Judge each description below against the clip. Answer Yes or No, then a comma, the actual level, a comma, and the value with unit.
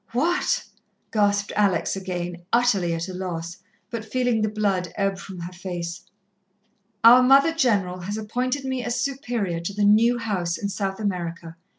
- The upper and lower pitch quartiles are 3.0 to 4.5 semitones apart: No, average, 4.9 semitones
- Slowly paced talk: No, average, 160 wpm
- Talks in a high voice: Yes, high, 200 Hz